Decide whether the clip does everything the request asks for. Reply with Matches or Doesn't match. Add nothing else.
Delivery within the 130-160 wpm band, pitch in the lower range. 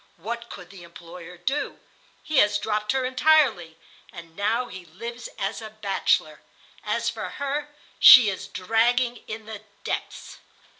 Doesn't match